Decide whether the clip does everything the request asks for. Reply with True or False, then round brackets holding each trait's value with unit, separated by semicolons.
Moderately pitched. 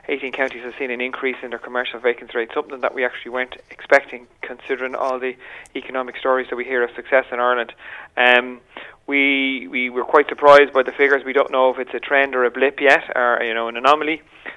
False (130 Hz)